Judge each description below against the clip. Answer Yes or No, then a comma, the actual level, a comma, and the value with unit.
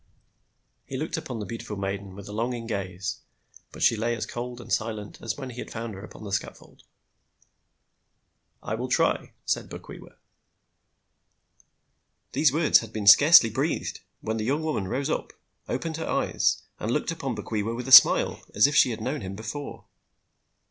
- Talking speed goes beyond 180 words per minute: No, average, 175 wpm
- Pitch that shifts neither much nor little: Yes, average, 4.0 semitones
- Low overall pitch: Yes, low, 115 Hz